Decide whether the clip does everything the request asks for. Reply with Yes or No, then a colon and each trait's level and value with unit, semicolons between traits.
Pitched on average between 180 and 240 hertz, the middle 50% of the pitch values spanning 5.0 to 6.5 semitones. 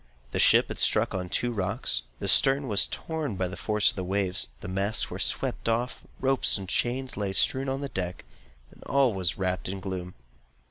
No: low, 100 Hz; wide, 5.5 semitones